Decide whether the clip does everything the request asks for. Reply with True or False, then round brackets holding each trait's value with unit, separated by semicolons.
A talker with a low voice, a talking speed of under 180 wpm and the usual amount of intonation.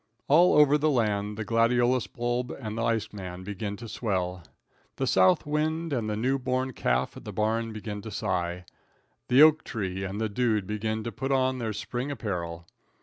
False (110 Hz; 190 wpm; 4.0 semitones)